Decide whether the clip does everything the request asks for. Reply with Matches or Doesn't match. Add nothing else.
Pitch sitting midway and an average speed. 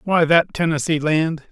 Matches